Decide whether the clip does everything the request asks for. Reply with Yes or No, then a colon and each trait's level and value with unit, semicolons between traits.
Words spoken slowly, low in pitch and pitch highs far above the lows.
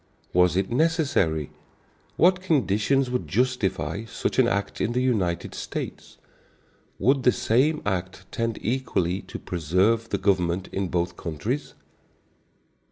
Yes: slow, 125 wpm; low, 110 Hz; wide, 5.8 semitones